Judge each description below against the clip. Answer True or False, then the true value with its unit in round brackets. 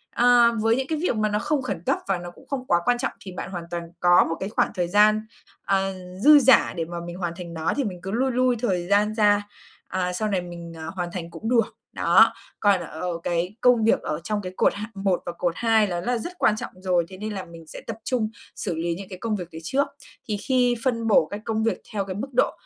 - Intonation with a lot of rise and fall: False (4.5 semitones)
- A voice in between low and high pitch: False (200 Hz)